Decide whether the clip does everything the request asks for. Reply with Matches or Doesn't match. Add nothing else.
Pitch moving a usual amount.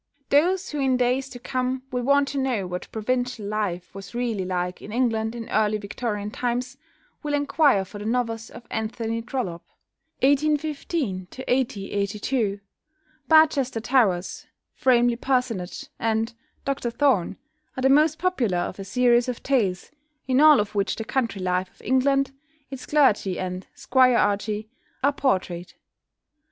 Matches